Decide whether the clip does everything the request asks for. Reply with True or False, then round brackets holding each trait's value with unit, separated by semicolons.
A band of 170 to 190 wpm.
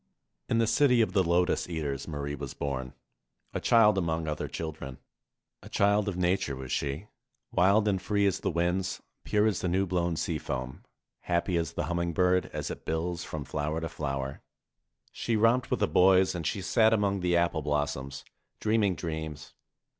True (180 wpm)